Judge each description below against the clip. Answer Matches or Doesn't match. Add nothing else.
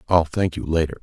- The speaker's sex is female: Doesn't match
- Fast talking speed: Matches